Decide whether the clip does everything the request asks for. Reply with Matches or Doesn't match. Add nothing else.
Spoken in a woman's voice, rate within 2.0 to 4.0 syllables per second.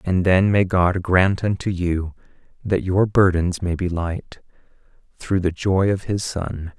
Doesn't match